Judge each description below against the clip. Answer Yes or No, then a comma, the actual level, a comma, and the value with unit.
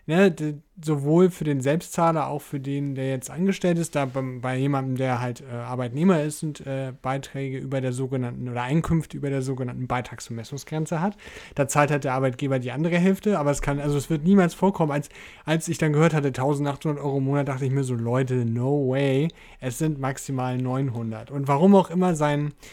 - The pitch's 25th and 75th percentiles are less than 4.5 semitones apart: Yes, average, 3.1 semitones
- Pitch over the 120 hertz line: Yes, medium, 140 Hz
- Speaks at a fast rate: Yes, fast, 200 wpm